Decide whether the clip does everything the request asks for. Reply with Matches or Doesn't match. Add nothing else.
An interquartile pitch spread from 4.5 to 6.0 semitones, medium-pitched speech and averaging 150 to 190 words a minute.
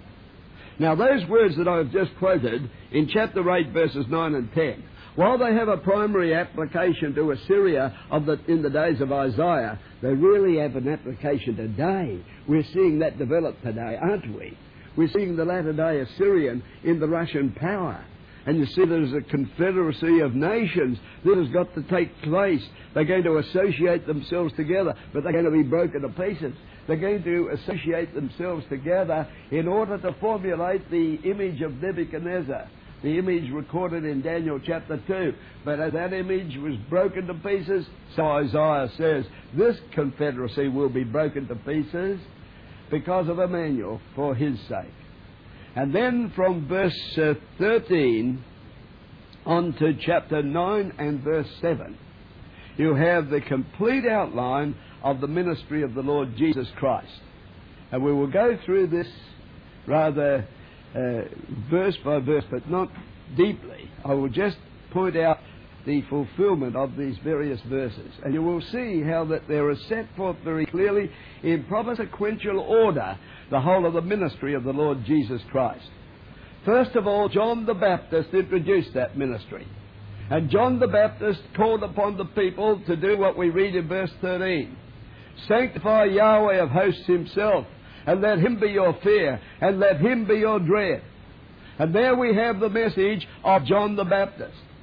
Matches